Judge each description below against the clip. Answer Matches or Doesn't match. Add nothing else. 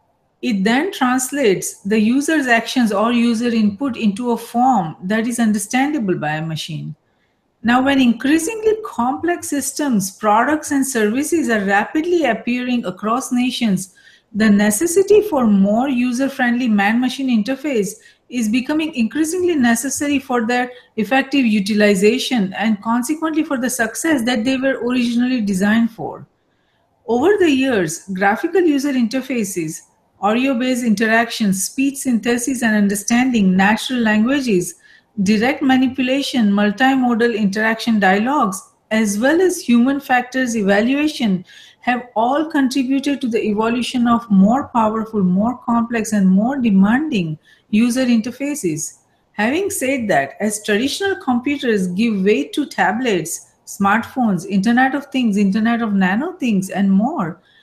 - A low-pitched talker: Doesn't match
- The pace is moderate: Doesn't match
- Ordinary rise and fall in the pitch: Matches